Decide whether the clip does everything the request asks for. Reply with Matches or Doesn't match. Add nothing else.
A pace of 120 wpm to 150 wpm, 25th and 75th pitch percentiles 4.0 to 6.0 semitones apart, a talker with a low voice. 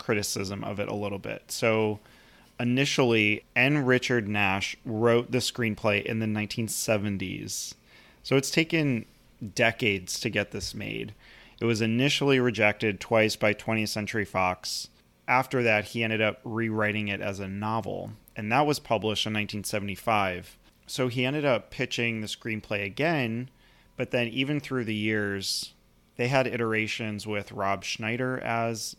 Doesn't match